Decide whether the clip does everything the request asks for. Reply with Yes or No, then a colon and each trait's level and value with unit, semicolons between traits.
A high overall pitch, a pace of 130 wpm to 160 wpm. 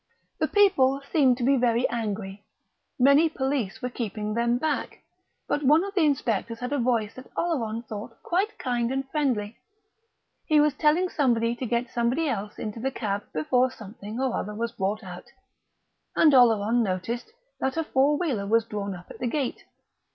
No: high, 240 Hz; average, 175 wpm